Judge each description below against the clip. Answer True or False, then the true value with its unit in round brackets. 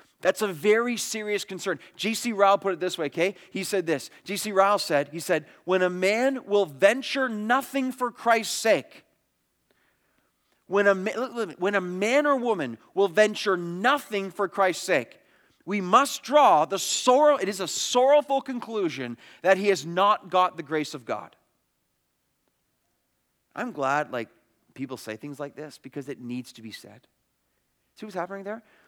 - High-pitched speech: True (195 Hz)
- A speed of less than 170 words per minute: True (160 wpm)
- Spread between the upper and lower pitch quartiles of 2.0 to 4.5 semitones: False (4.9 semitones)